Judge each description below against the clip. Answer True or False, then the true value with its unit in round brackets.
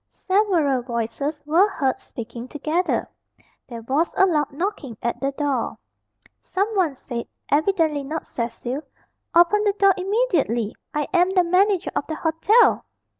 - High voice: True (310 Hz)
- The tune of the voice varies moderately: False (5.9 semitones)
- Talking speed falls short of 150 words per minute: True (135 wpm)